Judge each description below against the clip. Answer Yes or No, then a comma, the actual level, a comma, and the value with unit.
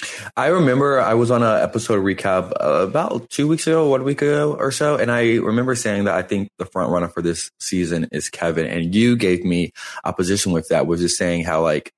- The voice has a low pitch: Yes, low, 100 Hz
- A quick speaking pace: Yes, fast, 225 wpm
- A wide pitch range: Yes, wide, 6.6 semitones